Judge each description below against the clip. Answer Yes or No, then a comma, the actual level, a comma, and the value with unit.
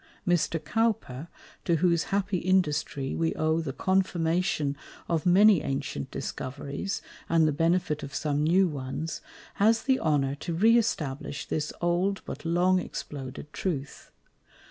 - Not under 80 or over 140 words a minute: Yes, slow, 135 wpm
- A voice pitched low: No, medium, 165 Hz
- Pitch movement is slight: No, average, 4.2 semitones